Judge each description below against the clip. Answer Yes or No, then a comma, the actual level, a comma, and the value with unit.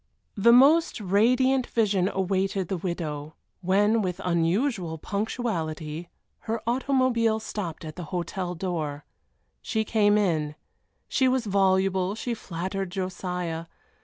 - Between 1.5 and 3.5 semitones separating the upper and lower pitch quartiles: No, average, 4.4 semitones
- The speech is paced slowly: Yes, slow, 115 wpm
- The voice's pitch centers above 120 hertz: Yes, high, 190 Hz